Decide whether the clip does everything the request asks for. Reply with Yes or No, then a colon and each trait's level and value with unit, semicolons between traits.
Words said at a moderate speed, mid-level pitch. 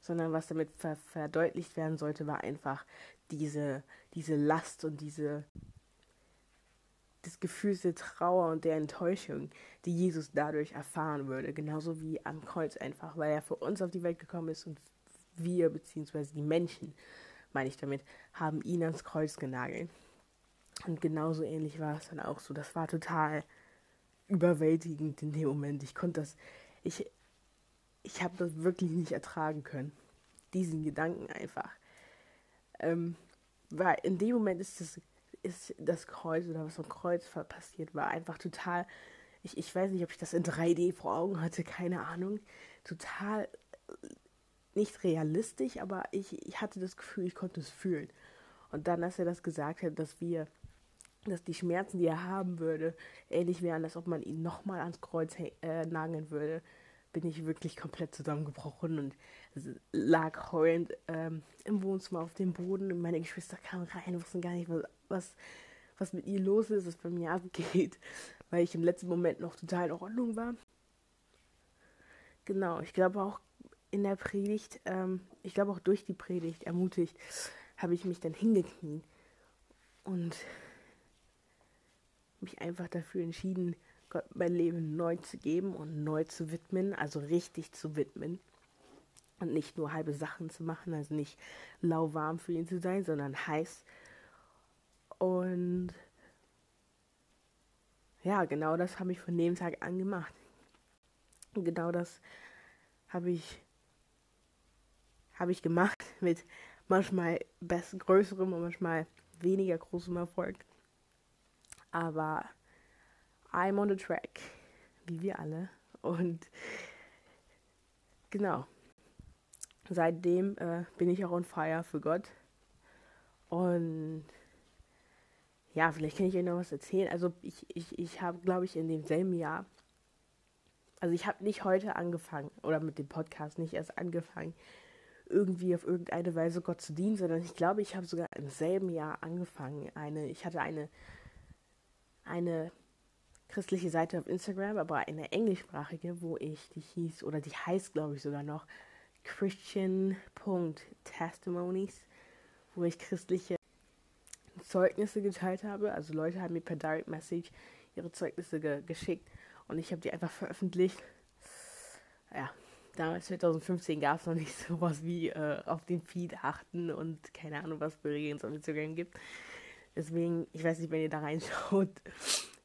Yes: average, 150 wpm; medium, 170 Hz